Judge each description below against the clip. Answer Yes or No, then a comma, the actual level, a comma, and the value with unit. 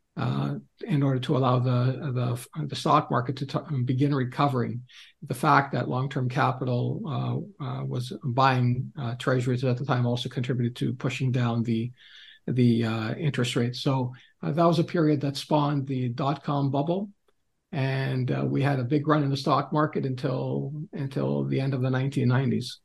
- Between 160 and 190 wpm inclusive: Yes, average, 175 wpm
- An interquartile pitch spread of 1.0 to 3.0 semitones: Yes, narrow, 2.5 semitones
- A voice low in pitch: Yes, low, 130 Hz